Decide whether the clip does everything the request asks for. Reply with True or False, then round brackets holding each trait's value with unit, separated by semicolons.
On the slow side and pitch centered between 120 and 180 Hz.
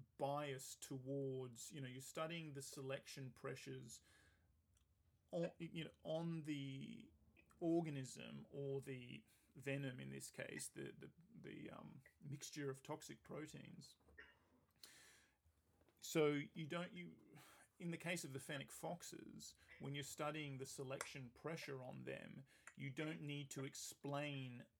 True (130 wpm; 140 Hz)